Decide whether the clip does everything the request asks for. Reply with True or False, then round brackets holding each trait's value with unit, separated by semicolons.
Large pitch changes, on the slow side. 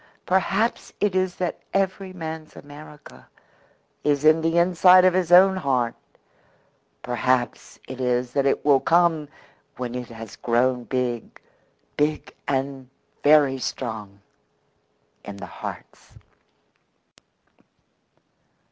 True (5.7 semitones; 110 wpm)